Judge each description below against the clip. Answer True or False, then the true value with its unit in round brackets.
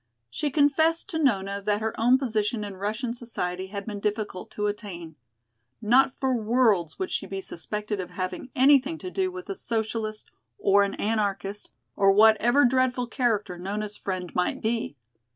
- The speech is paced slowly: False (165 wpm)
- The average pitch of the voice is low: False (215 Hz)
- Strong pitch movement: False (4.1 semitones)